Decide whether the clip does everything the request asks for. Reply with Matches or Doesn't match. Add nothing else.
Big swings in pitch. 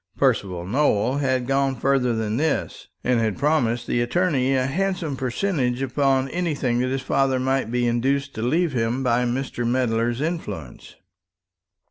Doesn't match